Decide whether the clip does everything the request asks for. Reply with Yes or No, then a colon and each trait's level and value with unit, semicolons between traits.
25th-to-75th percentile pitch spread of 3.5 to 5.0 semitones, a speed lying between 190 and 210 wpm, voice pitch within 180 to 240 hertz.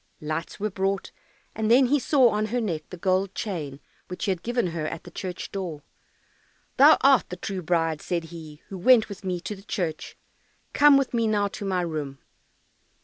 Yes: average, 4.6 semitones; average, 200 wpm; high, 190 Hz